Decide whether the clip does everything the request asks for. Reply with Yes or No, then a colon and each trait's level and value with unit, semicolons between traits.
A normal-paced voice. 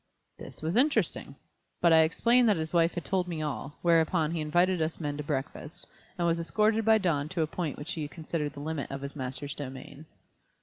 No: fast, 210 wpm